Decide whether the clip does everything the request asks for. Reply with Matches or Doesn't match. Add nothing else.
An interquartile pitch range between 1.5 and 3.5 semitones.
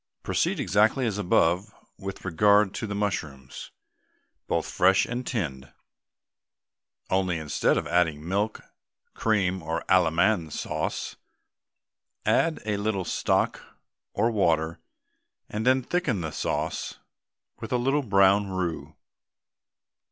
Doesn't match